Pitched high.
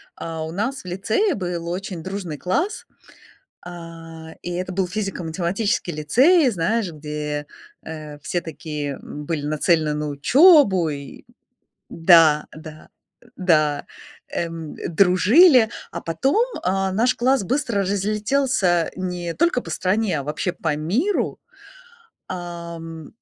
No: medium, 175 Hz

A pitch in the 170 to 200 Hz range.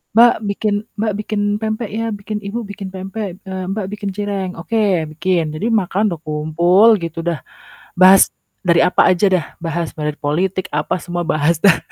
Yes: medium, 185 Hz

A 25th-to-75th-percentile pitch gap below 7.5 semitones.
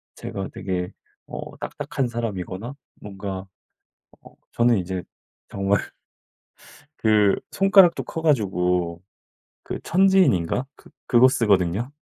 Yes: wide, 5.5 semitones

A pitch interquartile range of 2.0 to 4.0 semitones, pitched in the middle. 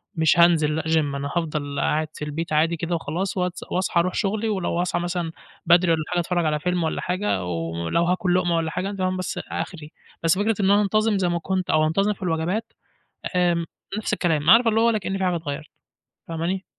Yes: average, 2.8 semitones; medium, 175 Hz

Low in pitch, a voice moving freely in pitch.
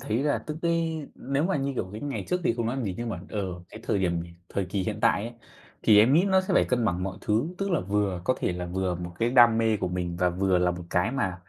Yes: low, 110 Hz; wide, 6.8 semitones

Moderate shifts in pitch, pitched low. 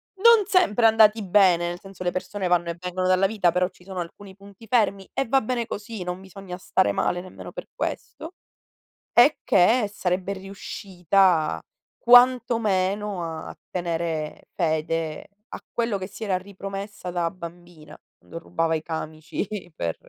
No: average, 3.2 semitones; medium, 185 Hz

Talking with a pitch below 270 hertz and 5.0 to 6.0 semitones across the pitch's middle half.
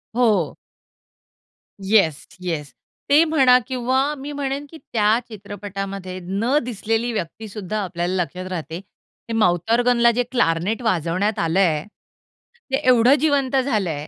Yes: high, 215 Hz; wide, 5.5 semitones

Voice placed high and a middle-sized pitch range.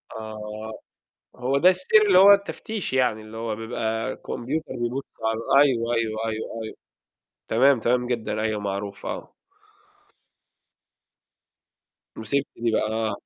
No: low, 115 Hz; average, 3.6 semitones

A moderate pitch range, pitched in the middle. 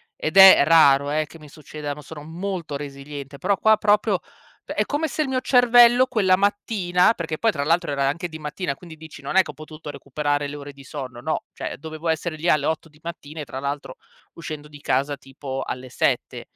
Yes: average, 4.3 semitones; medium, 155 Hz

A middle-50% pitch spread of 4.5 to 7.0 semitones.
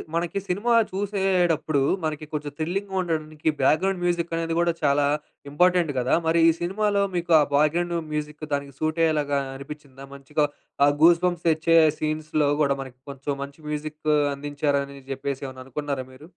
No: average, 3.2 semitones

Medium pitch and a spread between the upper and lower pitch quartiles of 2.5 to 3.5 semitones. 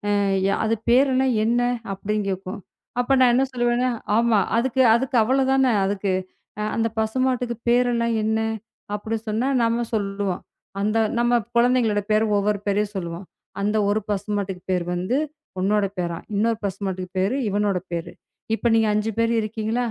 No: high, 220 Hz; average, 3.1 semitones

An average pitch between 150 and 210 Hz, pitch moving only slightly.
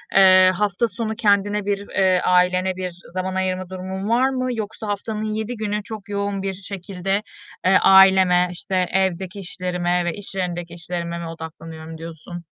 Yes: high, 190 Hz; narrow, 2.3 semitones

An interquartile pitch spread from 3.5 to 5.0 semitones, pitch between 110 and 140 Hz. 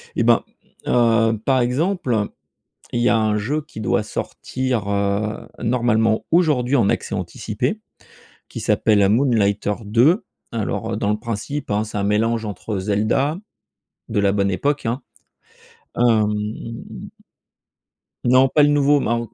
Yes: average, 3.8 semitones; low, 115 Hz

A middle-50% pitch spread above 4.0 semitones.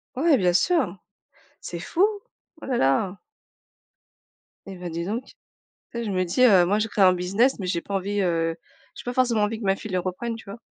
Yes: average, 4.5 semitones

